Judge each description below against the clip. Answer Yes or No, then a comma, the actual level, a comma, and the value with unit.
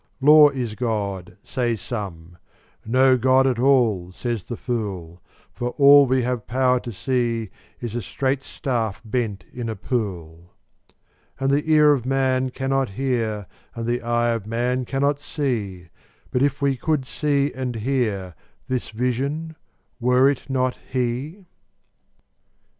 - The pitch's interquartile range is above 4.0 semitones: No, average, 3.2 semitones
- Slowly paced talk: Yes, slow, 130 wpm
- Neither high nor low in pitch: No, low, 125 Hz